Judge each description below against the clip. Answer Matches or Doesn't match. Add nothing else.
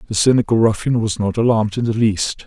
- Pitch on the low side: Matches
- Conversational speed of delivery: Doesn't match